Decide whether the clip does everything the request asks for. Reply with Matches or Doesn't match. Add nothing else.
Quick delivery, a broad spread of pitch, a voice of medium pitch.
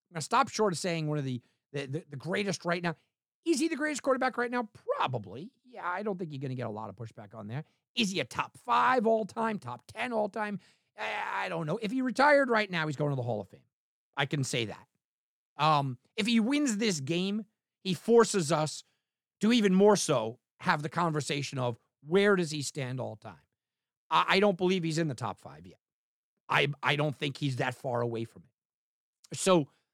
Matches